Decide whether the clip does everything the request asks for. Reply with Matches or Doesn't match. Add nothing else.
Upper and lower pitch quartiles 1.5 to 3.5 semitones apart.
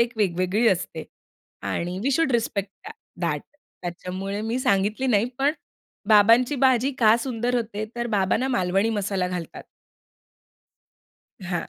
Doesn't match